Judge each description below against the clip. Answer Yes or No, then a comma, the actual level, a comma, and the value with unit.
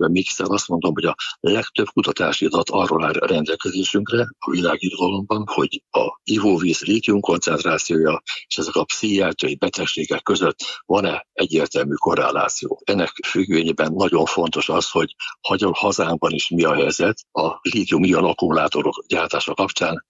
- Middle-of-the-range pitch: No, low, 100 Hz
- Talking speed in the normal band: Yes, average, 135 wpm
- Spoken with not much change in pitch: No, average, 3.2 semitones